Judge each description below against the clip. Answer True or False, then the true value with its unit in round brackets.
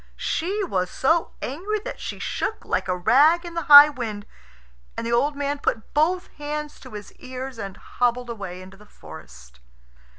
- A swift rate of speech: False (175 wpm)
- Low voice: False (260 Hz)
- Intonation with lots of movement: True (6.6 semitones)